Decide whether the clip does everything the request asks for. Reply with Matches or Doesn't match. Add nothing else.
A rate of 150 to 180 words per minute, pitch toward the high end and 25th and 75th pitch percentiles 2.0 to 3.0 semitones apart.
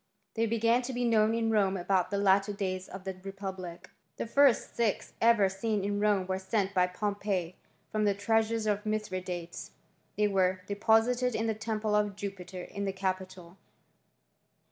Matches